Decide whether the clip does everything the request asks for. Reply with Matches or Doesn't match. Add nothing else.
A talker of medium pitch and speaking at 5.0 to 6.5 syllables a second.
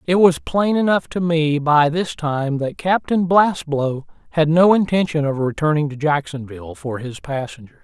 Doesn't match